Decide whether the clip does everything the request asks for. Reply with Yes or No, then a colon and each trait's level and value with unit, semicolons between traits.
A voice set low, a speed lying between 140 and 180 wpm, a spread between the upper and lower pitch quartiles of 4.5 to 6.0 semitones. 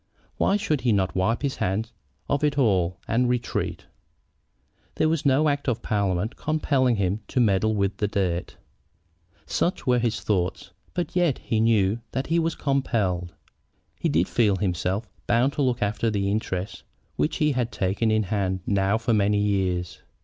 Yes: low, 110 Hz; average, 165 wpm; average, 5.0 semitones